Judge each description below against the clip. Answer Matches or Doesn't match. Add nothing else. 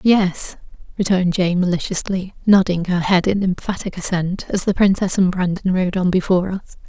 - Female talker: Matches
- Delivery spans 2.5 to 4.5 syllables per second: Doesn't match